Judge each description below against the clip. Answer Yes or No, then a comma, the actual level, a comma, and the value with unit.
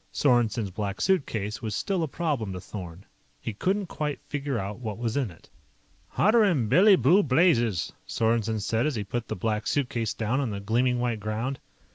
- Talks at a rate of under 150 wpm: No, average, 180 wpm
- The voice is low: Yes, low, 115 Hz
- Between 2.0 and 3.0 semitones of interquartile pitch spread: No, average, 5.2 semitones